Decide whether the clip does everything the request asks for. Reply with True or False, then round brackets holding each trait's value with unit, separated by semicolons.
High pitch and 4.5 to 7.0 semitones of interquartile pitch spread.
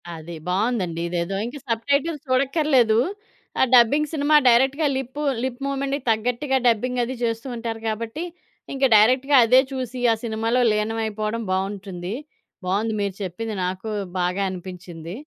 True (230 Hz; 4.8 semitones)